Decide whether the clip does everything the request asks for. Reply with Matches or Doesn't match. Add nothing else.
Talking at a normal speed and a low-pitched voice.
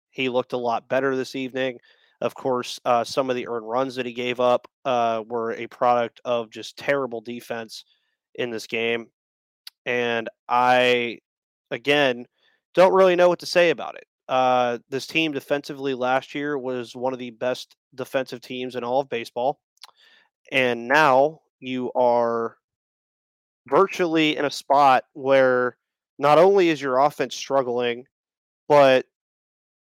Matches